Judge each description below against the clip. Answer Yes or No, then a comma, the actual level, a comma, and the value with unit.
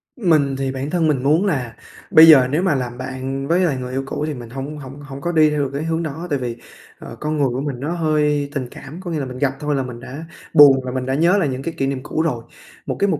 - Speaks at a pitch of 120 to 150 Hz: Yes, medium, 140 Hz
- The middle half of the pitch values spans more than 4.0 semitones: No, average, 3.0 semitones